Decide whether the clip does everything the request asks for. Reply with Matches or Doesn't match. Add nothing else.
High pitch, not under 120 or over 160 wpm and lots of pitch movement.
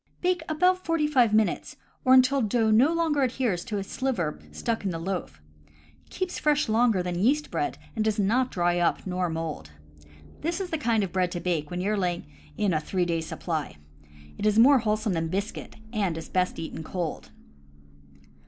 Doesn't match